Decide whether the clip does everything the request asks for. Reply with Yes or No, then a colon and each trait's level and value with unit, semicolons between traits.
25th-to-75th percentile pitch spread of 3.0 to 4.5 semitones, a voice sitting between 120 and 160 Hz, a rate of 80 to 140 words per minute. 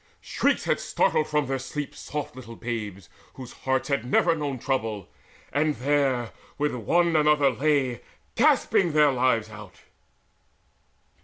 Yes: average, 3.9 semitones; low, 135 Hz; slow, 135 wpm